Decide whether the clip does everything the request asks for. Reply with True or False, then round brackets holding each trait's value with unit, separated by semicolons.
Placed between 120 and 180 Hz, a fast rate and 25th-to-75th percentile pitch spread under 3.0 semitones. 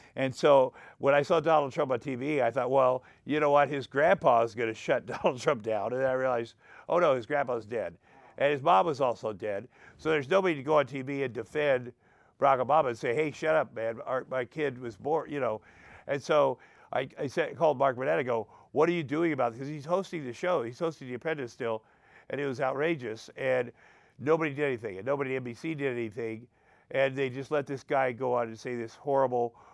False (135 Hz; 230 wpm; 3.6 semitones)